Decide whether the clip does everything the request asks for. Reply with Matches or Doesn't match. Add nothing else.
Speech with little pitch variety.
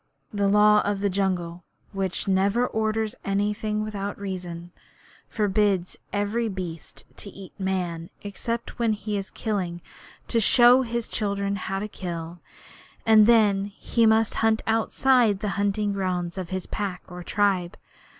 Matches